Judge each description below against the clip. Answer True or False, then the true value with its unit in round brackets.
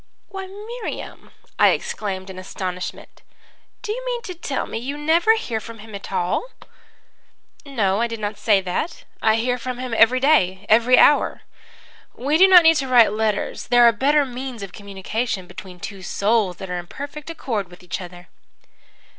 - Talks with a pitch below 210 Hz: False (230 Hz)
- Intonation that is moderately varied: False (6.8 semitones)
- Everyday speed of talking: True (180 wpm)